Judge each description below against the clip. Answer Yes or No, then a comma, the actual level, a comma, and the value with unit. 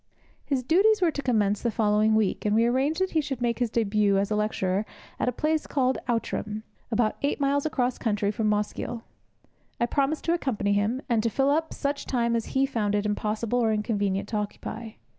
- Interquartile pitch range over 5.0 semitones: No, average, 4.5 semitones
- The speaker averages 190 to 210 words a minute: Yes, fast, 205 wpm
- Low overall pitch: No, high, 230 Hz